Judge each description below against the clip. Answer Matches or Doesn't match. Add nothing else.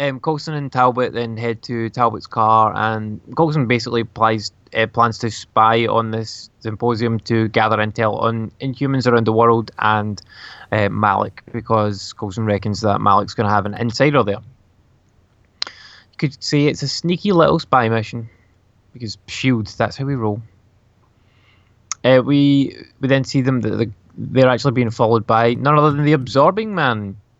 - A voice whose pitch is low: Matches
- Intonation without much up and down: Doesn't match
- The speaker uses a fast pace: Doesn't match